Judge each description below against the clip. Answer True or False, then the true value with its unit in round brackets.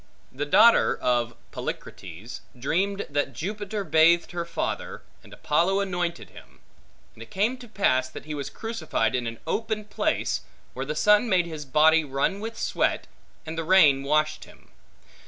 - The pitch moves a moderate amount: False (6.0 semitones)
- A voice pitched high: False (160 Hz)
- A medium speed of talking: True (160 wpm)